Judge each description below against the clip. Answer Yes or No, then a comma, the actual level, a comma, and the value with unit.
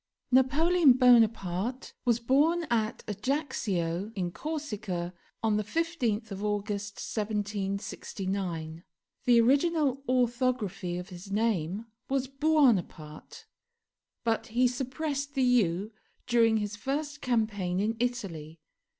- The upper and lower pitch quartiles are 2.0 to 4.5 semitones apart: No, average, 4.9 semitones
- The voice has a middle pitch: No, high, 225 Hz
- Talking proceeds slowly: Yes, slow, 105 wpm